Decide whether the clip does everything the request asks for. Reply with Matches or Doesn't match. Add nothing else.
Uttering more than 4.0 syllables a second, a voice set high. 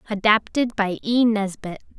Matches